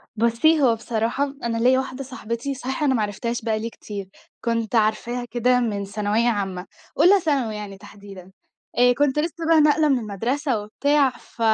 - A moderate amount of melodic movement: Yes, average, 4.1 semitones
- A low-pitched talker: No, high, 235 Hz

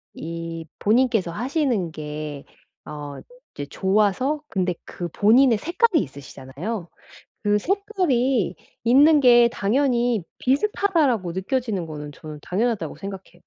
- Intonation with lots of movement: Yes, wide, 7.7 semitones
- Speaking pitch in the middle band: No, high, 210 Hz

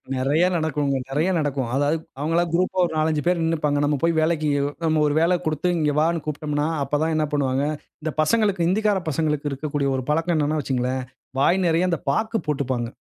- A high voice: No, medium, 155 Hz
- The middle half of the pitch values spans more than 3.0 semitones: No, average, 2.7 semitones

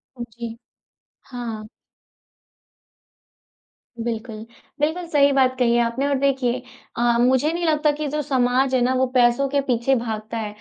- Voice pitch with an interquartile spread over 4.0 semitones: No, average, 2.7 semitones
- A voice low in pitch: No, very high, 255 Hz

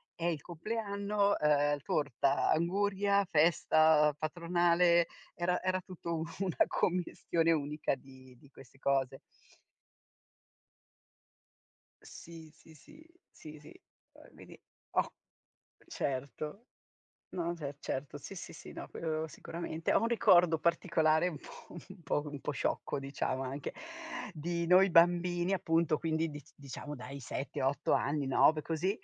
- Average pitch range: Yes, average, 3.2 semitones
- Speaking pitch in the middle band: Yes, medium, 160 Hz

